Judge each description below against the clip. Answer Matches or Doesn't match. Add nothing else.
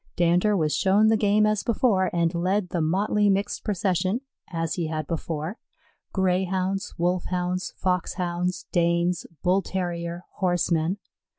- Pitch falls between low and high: Matches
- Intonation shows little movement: Matches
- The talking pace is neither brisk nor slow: Doesn't match